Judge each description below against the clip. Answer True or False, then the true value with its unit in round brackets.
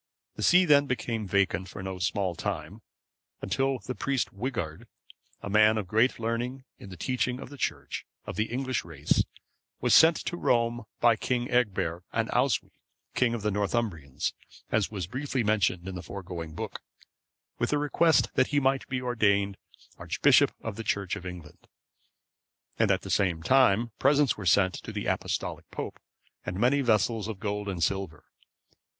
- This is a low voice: True (110 Hz)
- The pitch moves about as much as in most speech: True (4.8 semitones)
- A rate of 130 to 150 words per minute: False (170 wpm)